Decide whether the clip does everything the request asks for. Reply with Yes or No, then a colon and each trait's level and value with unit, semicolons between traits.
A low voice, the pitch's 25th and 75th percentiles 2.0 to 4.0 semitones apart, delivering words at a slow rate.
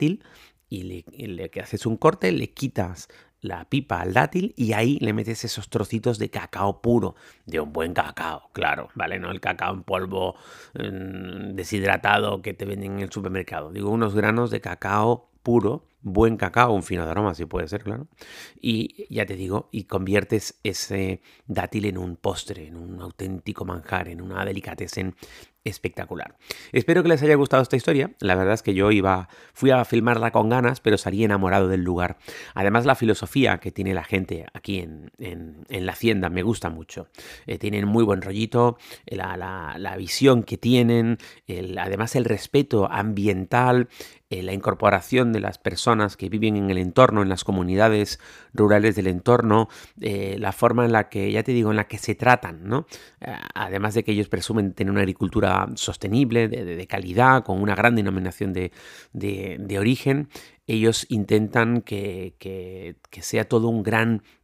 No: low, 105 Hz; average, 3.4 semitones; average, 180 wpm